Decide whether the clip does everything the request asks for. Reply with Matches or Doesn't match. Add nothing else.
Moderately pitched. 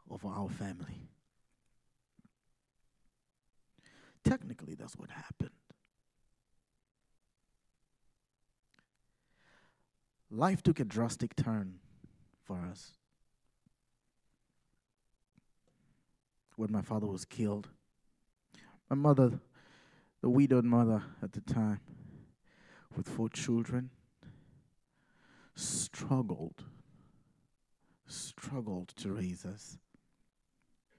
Doesn't match